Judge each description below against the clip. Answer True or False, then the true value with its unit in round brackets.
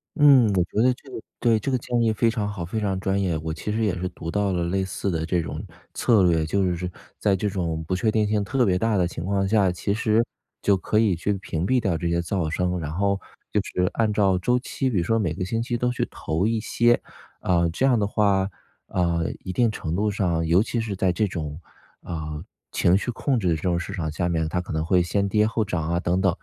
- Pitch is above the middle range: False (95 Hz)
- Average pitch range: True (3.9 semitones)